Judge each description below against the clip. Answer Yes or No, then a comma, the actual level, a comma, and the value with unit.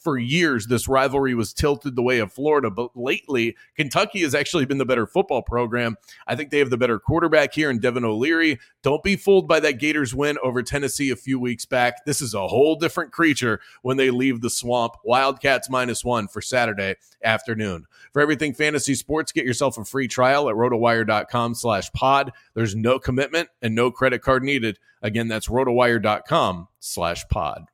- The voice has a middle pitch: No, low, 125 Hz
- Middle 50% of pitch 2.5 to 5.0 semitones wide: Yes, average, 3.4 semitones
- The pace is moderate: Yes, average, 180 wpm